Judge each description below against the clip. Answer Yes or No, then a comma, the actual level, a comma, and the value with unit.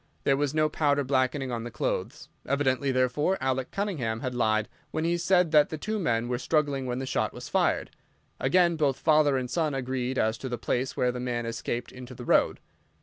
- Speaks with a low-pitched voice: Yes, low, 130 Hz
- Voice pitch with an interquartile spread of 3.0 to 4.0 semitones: Yes, average, 3.5 semitones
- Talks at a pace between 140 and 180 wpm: No, fast, 205 wpm